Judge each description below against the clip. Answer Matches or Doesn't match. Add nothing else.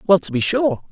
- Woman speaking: Doesn't match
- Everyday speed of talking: Doesn't match